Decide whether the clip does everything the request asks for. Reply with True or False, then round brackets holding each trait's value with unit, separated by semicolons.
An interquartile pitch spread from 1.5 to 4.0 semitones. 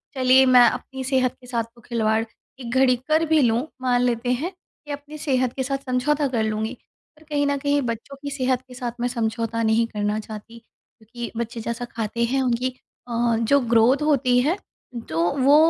True (2.7 semitones)